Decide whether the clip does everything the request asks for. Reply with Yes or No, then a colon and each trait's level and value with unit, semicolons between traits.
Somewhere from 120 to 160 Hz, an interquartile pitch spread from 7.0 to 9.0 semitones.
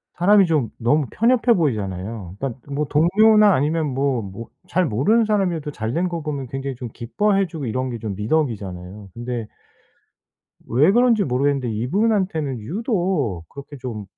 Yes: medium, 140 Hz; wide, 7.8 semitones